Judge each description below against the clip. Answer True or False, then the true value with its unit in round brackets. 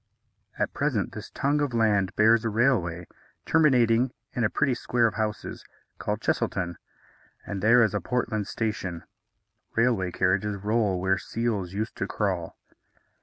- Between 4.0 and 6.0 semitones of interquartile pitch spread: False (3.6 semitones)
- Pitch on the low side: True (110 Hz)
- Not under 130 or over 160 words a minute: True (145 wpm)